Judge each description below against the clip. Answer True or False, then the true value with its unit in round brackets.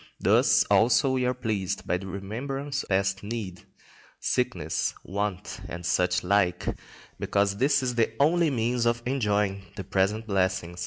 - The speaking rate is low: False (150 wpm)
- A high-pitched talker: False (105 Hz)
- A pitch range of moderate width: True (4.6 semitones)